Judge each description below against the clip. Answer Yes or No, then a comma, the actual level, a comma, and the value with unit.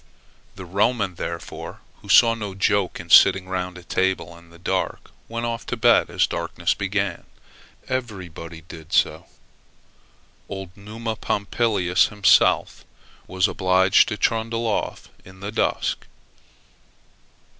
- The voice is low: Yes, very low, 95 Hz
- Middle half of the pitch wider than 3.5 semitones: No, average, 3.2 semitones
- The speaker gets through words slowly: Yes, slow, 130 wpm